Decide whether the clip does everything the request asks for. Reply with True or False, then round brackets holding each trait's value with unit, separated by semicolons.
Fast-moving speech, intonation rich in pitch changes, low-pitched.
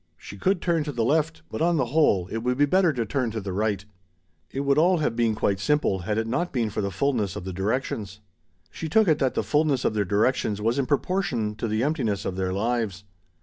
True (240 wpm; 6.2 semitones; 120 Hz)